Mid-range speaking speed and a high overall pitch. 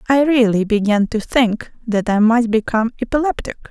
Yes: average, 160 wpm; high, 230 Hz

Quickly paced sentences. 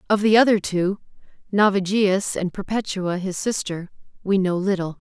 No: average, 140 wpm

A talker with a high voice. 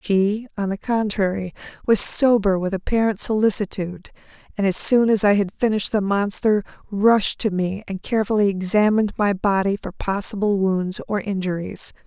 Yes: high, 200 Hz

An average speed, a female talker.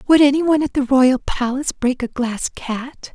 Yes: average, 190 wpm; female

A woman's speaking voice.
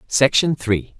No: male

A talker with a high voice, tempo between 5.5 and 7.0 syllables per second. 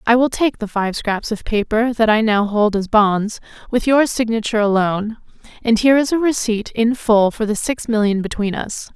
No: high, 220 Hz; 5.1 syllables/s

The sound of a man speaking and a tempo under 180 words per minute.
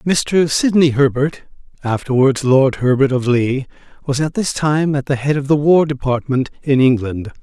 Yes: male; average, 170 wpm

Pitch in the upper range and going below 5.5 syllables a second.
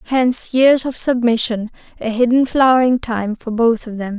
Yes: high, 240 Hz; 4.9 syllables/s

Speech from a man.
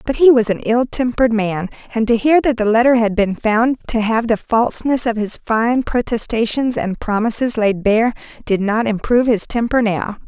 No: female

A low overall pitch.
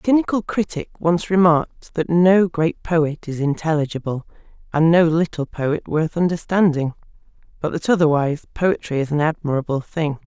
No: medium, 160 Hz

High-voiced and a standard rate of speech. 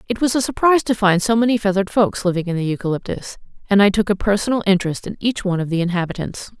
No: high, 200 Hz; fast, 235 wpm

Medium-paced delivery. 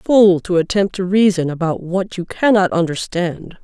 Yes: average, 165 wpm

